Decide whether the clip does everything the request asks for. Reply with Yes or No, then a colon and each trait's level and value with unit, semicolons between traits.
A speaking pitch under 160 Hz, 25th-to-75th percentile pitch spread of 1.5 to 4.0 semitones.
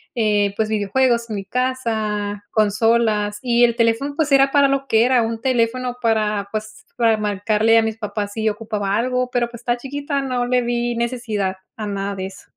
No: high, 230 Hz; average, 2.8 semitones